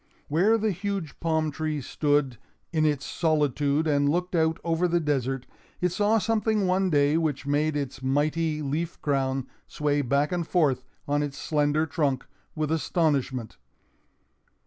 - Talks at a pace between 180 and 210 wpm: No, average, 145 wpm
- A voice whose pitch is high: No, medium, 150 Hz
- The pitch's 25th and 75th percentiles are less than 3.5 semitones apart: Yes, average, 2.8 semitones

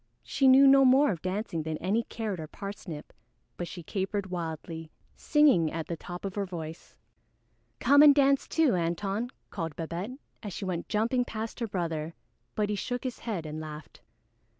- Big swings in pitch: Yes, wide, 6.0 semitones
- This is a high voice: Yes, high, 195 Hz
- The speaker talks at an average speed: Yes, average, 175 wpm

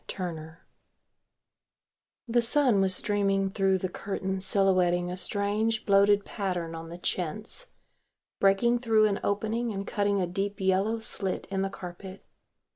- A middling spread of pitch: No, narrow, 2.1 semitones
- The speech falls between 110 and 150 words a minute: Yes, slow, 135 wpm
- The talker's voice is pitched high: Yes, high, 195 Hz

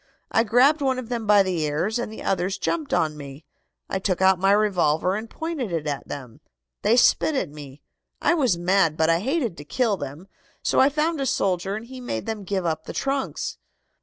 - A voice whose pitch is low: No, high, 195 Hz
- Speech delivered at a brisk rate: Yes, fast, 215 wpm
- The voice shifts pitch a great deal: Yes, wide, 7.0 semitones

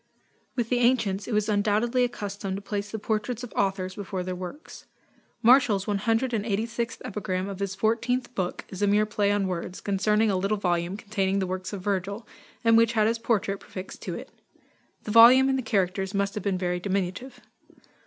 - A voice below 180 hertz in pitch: No, high, 205 Hz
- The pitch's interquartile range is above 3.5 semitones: No, average, 2.9 semitones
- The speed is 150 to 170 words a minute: No, average, 190 wpm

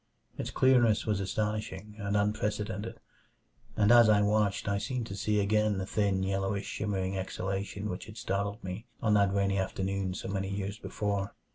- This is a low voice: Yes, low, 100 Hz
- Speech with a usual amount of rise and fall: No, narrow, 1.5 semitones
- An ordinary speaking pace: Yes, average, 165 wpm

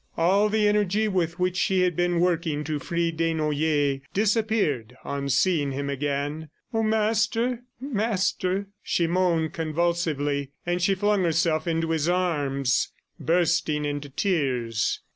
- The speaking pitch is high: No, medium, 170 Hz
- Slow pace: Yes, slow, 130 wpm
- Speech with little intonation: No, average, 4.4 semitones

